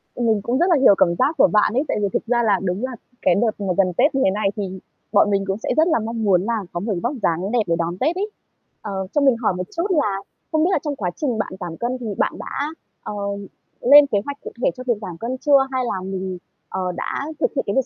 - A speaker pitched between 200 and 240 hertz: Yes, high, 225 Hz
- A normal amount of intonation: No, wide, 5.7 semitones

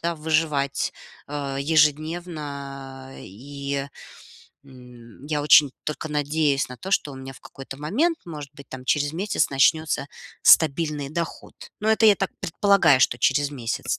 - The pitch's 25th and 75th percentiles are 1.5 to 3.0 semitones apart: Yes, average, 2.7 semitones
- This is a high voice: No, medium, 145 Hz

